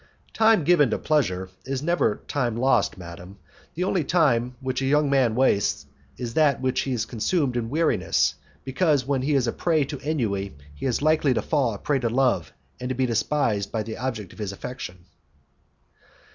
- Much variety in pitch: No, average, 4.5 semitones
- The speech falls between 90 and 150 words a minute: No, average, 185 wpm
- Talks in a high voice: No, low, 130 Hz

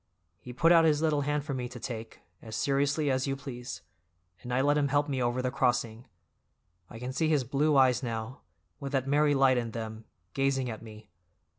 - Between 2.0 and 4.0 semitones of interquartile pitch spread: Yes, average, 2.8 semitones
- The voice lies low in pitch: Yes, low, 130 Hz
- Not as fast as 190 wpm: No, fast, 205 wpm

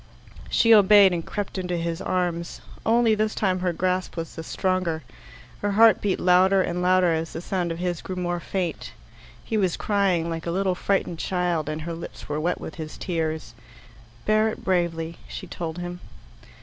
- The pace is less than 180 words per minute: No, average, 185 wpm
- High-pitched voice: No, medium, 180 Hz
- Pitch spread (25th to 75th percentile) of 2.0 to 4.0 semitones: Yes, narrow, 2.4 semitones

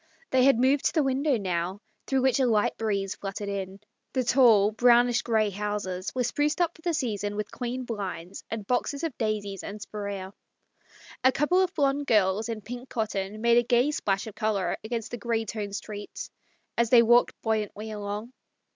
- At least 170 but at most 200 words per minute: Yes, average, 190 wpm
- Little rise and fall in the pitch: No, average, 3.7 semitones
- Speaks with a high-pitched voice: Yes, high, 220 Hz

